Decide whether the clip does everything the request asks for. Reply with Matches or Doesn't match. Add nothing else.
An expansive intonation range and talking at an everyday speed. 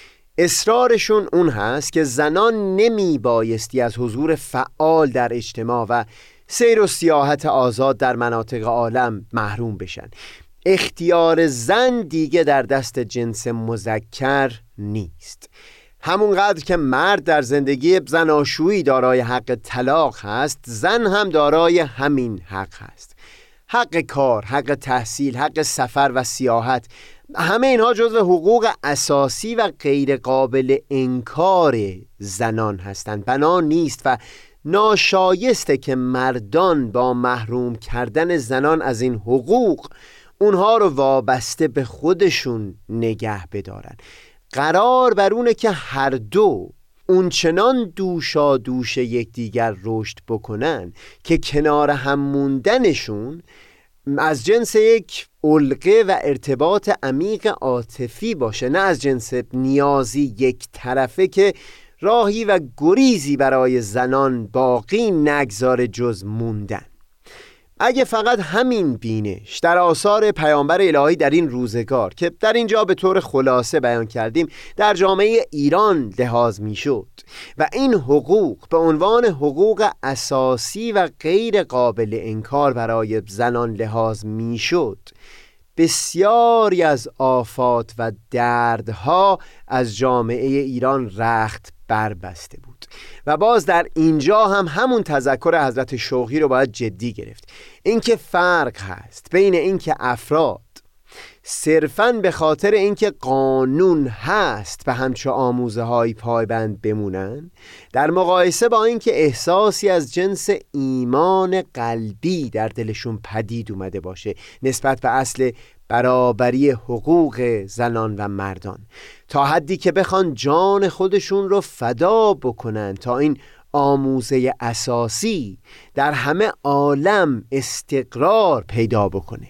Matches